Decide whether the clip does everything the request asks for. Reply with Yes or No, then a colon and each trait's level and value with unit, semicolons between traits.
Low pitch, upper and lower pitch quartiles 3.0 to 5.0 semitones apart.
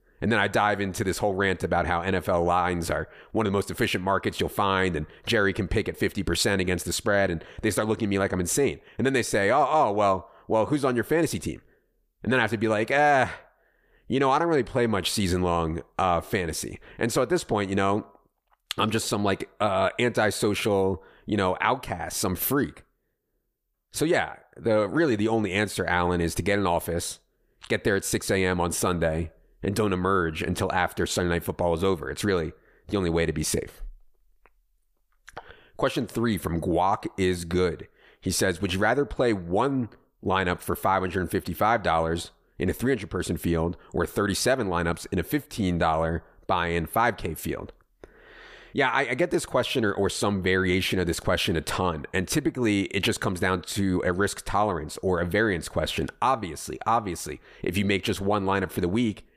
Yes: very low, 95 Hz; average, 3.4 semitones